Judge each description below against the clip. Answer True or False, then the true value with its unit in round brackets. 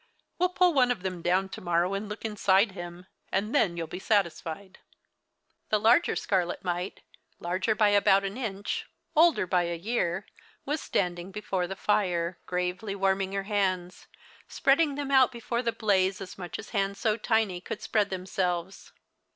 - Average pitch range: True (3.4 semitones)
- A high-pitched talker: True (195 Hz)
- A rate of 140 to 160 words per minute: False (175 wpm)